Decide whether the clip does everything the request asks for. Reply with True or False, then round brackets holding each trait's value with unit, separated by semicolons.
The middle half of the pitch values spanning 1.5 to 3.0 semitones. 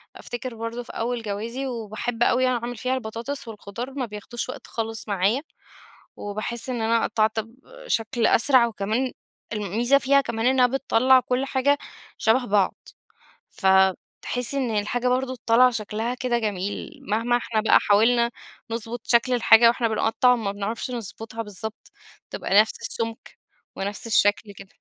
True (2.5 semitones)